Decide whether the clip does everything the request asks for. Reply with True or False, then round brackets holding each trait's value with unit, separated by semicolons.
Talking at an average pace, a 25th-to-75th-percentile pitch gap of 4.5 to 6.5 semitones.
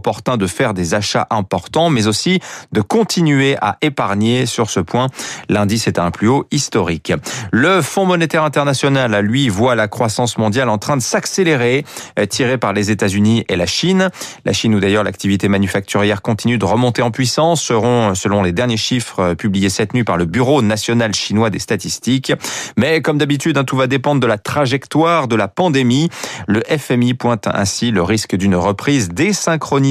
True (180 wpm; 5.2 semitones)